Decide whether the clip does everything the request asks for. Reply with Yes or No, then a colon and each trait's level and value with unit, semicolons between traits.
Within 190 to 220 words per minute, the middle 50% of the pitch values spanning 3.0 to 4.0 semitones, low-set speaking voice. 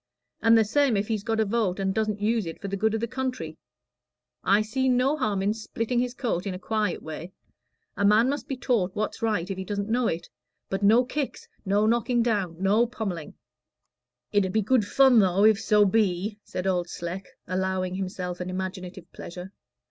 No: average, 200 wpm; average, 3.4 semitones; high, 210 Hz